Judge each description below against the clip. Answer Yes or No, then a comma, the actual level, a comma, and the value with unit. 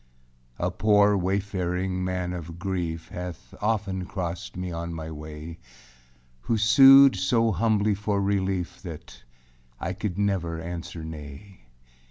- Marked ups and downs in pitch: No, average, 3.2 semitones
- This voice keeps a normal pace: No, slow, 125 wpm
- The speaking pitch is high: No, very low, 90 Hz